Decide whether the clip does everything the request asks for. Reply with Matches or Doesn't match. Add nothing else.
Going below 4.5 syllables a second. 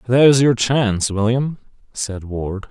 Matches